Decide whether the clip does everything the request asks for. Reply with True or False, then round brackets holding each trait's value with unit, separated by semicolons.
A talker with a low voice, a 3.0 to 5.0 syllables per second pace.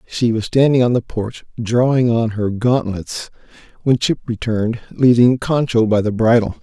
True (115 Hz; 4.7 syllables/s)